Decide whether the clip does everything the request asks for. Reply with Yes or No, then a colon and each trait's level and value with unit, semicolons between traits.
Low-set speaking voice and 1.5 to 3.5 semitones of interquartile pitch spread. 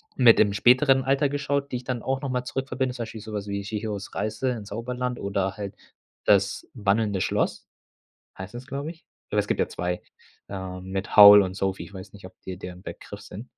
No: low, 110 Hz; average, 4.4 semitones